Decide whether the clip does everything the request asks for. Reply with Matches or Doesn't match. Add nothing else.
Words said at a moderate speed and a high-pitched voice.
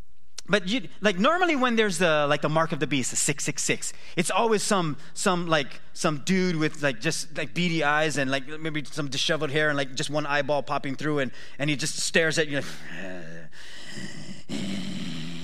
Doesn't match